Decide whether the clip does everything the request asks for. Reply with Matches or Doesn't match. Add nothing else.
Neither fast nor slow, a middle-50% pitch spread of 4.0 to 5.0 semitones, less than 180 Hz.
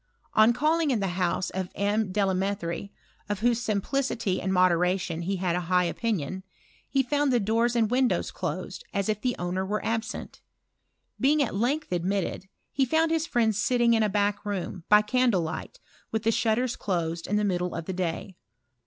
Doesn't match